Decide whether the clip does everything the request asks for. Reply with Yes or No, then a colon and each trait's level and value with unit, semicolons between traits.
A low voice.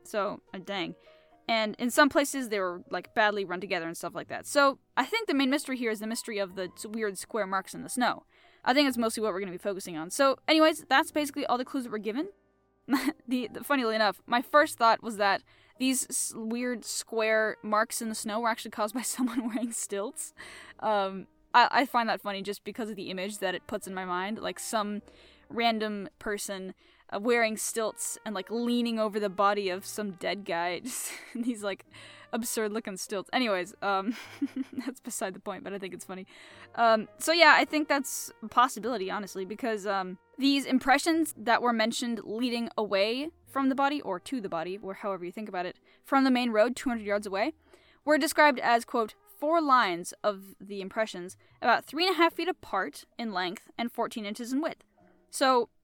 No: high, 225 Hz